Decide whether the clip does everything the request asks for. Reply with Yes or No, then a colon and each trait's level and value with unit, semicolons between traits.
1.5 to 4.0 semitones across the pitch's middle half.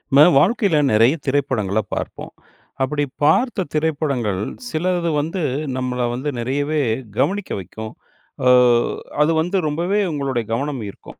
No: average, 4.8 semitones